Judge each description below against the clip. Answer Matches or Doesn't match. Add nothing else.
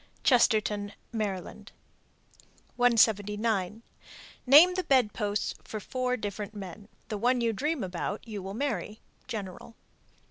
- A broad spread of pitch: Doesn't match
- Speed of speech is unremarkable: Doesn't match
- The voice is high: Matches